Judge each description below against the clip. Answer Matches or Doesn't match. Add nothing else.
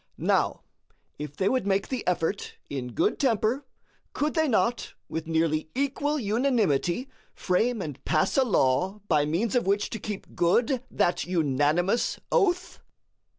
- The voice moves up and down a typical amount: Doesn't match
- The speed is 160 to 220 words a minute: Doesn't match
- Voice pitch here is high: Matches